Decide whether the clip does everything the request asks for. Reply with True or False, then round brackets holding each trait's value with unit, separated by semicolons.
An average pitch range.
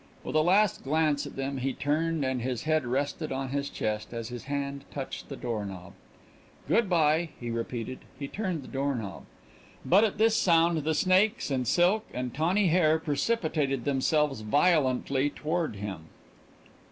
True (4.3 semitones)